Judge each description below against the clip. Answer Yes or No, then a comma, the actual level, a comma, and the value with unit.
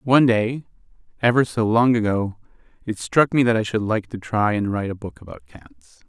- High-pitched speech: No, low, 110 Hz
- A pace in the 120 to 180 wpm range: No, fast, 205 wpm